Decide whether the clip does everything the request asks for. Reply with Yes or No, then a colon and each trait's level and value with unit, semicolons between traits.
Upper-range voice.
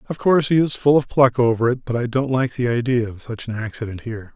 No: low, 125 Hz